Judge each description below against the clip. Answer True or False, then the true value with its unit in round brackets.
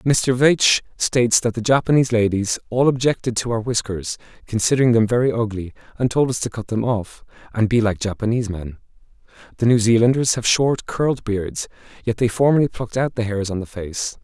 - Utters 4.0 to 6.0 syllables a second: True (5.6 syllables/s)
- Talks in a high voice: False (115 Hz)